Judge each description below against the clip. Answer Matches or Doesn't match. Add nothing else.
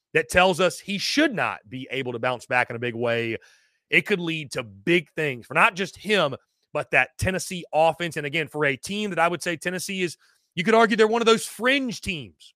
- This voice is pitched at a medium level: Matches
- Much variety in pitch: Matches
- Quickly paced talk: Matches